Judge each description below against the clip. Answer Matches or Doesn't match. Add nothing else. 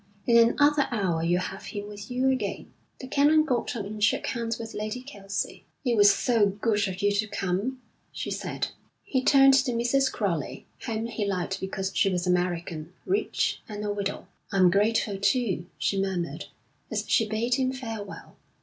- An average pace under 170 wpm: Doesn't match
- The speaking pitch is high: Matches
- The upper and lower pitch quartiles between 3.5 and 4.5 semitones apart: Matches